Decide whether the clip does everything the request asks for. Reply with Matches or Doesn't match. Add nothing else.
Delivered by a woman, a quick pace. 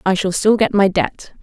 Matches